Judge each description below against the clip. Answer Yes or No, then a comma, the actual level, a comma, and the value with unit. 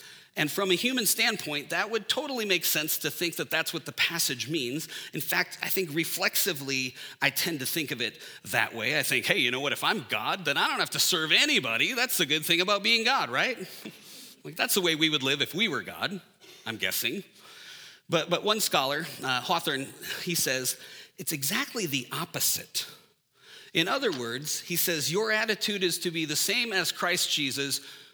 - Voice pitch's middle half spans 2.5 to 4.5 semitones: No, wide, 5.4 semitones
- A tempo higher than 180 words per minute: Yes, fast, 205 wpm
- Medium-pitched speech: Yes, medium, 175 Hz